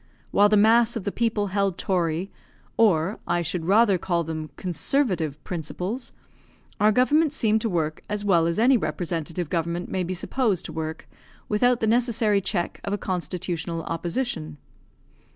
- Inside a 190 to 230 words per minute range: No, average, 155 wpm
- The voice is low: No, medium, 185 Hz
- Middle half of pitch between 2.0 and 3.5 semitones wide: No, average, 4.6 semitones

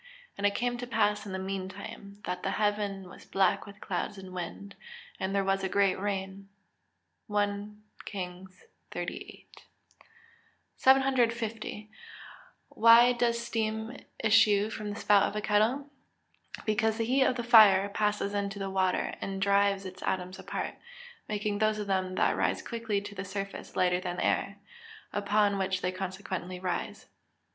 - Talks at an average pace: Yes, average, 155 wpm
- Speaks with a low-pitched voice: No, high, 200 Hz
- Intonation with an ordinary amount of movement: No, narrow, 2.1 semitones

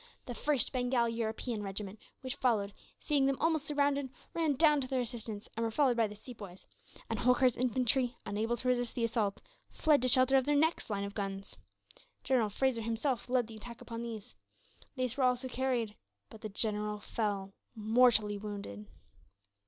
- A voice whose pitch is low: No, high, 235 Hz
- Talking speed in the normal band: Yes, average, 175 wpm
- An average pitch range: Yes, average, 3.5 semitones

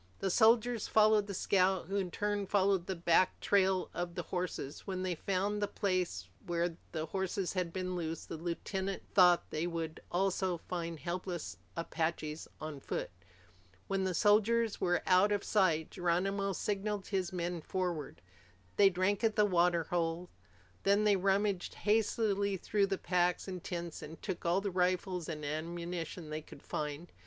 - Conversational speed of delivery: Yes, average, 165 wpm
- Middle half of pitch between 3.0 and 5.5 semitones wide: No, narrow, 2.6 semitones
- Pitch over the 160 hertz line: Yes, medium, 185 Hz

